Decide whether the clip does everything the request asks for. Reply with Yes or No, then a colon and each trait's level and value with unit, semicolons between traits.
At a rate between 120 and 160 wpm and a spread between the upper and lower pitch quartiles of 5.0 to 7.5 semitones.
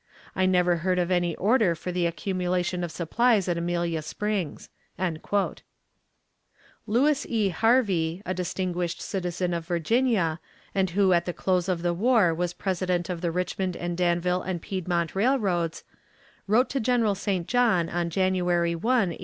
No: average, 155 wpm; narrow, 2.4 semitones